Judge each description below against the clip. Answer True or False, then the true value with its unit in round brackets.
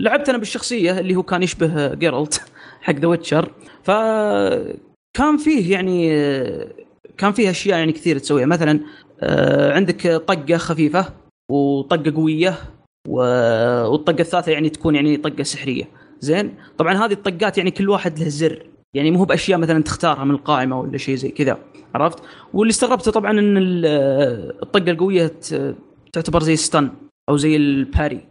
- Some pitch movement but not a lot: True (4.5 semitones)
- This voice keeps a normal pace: False (140 wpm)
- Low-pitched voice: False (165 Hz)